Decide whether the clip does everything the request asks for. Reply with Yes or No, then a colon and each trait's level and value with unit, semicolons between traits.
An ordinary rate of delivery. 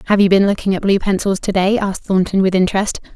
No: fast, 250 wpm